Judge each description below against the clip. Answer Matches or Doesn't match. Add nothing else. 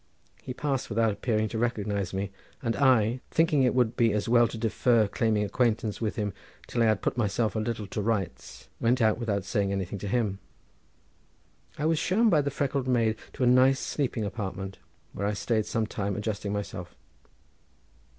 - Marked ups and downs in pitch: Doesn't match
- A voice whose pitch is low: Matches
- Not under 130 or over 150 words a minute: Doesn't match